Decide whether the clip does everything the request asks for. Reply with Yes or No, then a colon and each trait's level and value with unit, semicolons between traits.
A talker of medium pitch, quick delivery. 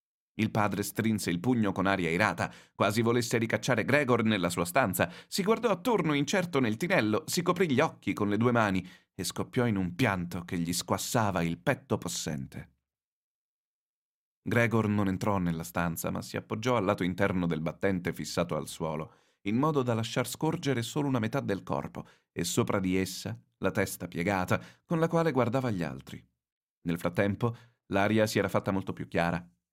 No: low, 105 Hz; fast, 180 wpm